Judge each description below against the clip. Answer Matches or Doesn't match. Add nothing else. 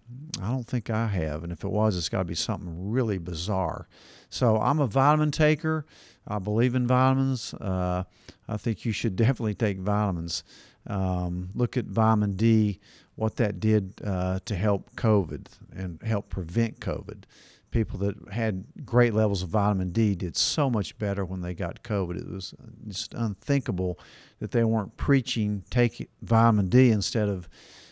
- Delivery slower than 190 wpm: Matches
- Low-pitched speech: Matches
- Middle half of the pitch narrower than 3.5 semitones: Doesn't match